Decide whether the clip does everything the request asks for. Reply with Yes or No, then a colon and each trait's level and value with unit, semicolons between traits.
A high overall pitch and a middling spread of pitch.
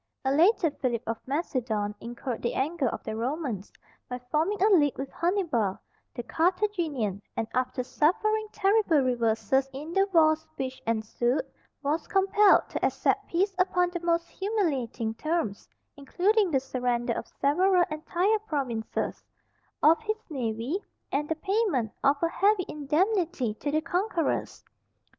No: very high, 305 Hz; wide, 6.7 semitones